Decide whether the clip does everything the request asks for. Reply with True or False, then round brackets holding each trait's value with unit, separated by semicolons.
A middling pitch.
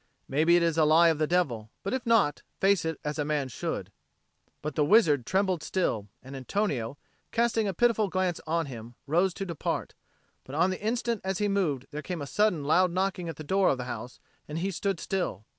True (170 Hz)